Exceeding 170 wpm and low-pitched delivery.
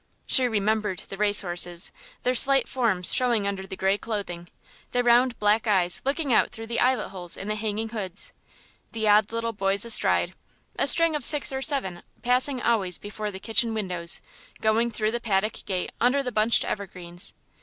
No: average, 180 wpm; high, 215 Hz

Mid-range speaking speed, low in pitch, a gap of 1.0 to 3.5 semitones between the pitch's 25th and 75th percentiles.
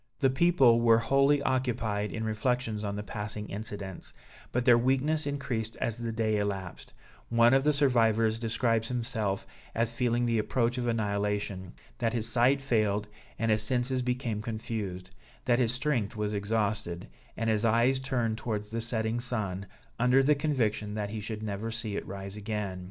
Yes: average, 170 wpm; low, 115 Hz; average, 2.9 semitones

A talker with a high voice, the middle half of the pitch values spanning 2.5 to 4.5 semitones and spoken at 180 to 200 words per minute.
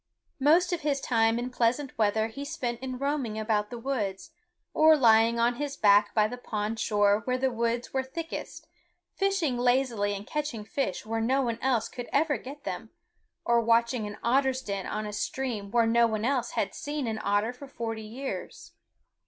Yes: high, 235 Hz; average, 3.5 semitones; average, 185 wpm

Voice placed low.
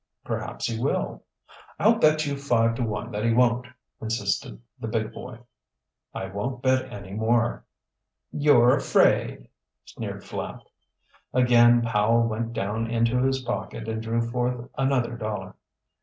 Yes: low, 115 Hz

